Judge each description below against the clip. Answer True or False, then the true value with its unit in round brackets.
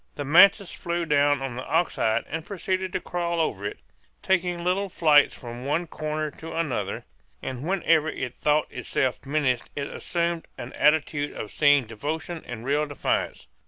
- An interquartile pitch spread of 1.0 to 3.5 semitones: False (4.1 semitones)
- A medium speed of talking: True (165 wpm)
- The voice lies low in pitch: False (150 Hz)